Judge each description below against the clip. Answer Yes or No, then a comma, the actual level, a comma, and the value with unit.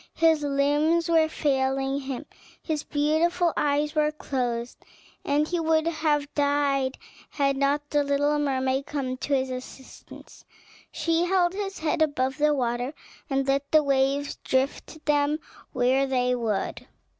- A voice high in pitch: Yes, very high, 285 Hz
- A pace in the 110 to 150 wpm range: Yes, average, 140 wpm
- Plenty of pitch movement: No, narrow, 2.4 semitones